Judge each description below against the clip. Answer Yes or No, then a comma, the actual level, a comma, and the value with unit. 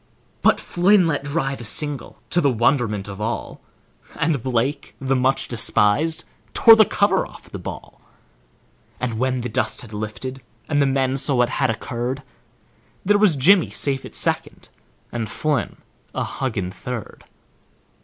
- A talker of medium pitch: No, low, 130 Hz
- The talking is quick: No, average, 150 wpm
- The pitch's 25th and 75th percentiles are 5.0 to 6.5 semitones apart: No, average, 3.8 semitones